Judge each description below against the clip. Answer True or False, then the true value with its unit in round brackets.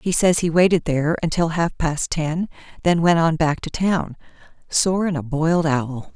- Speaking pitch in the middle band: True (165 Hz)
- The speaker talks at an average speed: True (185 wpm)